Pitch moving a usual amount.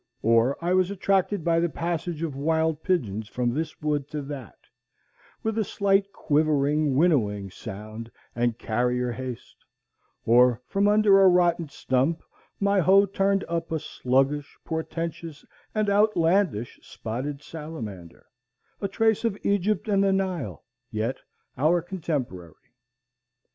No: wide, 7.2 semitones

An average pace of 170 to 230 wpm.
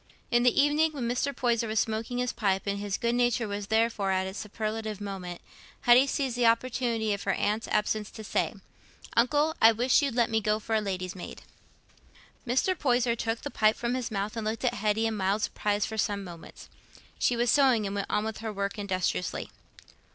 Yes: fast, 205 wpm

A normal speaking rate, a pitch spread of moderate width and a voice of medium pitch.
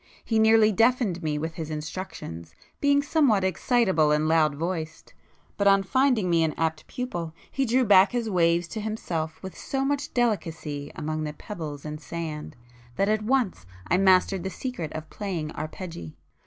No: average, 165 wpm; wide, 5.9 semitones; medium, 180 Hz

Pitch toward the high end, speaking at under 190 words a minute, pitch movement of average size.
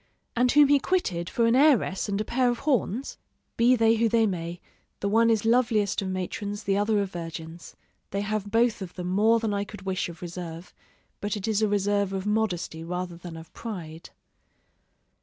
No: high, 205 Hz; average, 195 wpm; average, 3.9 semitones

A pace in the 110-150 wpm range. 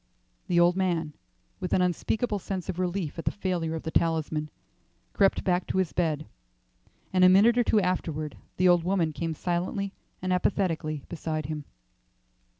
No: average, 165 wpm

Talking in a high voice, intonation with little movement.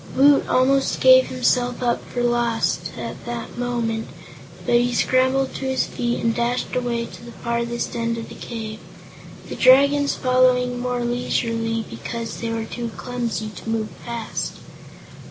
Yes: high, 240 Hz; narrow, 1.6 semitones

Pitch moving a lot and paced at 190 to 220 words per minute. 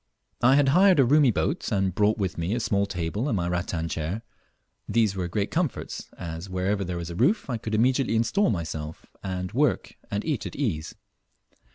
Yes: wide, 6.1 semitones; average, 195 wpm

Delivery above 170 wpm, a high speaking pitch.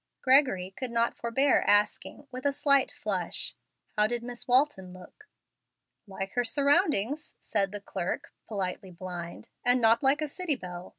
No: average, 155 wpm; high, 235 Hz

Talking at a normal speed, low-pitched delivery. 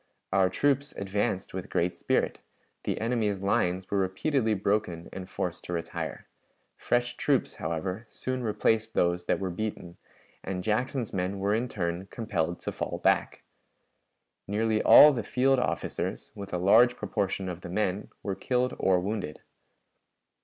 Yes: average, 150 wpm; low, 100 Hz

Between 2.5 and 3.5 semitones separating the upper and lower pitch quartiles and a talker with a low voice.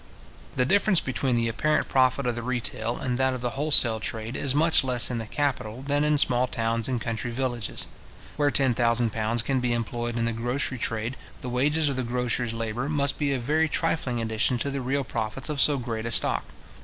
Yes: average, 3.0 semitones; low, 125 Hz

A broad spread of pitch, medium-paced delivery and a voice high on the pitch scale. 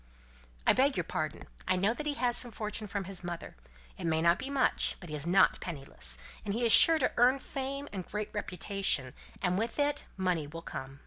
No: wide, 6.5 semitones; fast, 230 wpm; high, 195 Hz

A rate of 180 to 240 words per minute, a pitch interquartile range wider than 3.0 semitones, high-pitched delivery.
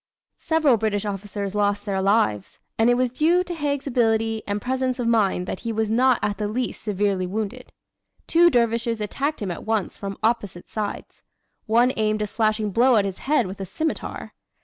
Yes: average, 190 wpm; average, 3.7 semitones; high, 220 Hz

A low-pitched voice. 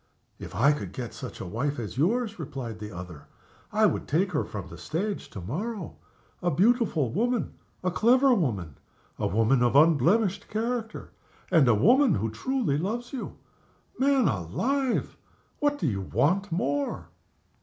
No: medium, 165 Hz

